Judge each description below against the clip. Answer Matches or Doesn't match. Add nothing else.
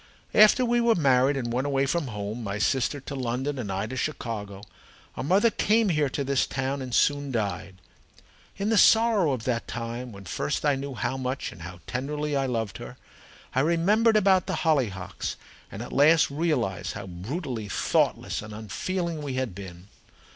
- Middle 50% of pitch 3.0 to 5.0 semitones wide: Doesn't match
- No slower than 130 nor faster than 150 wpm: Doesn't match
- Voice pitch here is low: Matches